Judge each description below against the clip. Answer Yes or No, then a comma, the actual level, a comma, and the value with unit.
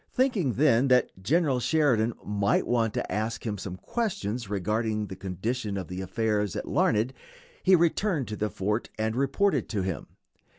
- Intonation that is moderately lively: Yes, average, 4.7 semitones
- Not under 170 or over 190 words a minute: No, average, 160 wpm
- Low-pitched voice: Yes, low, 110 Hz